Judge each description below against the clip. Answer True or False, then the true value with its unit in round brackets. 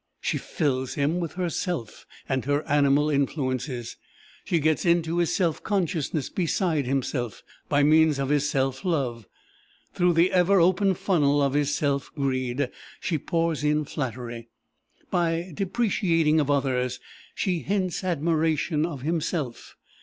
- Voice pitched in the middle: True (150 Hz)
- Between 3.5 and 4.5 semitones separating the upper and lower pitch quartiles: True (3.8 semitones)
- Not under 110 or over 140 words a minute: True (135 wpm)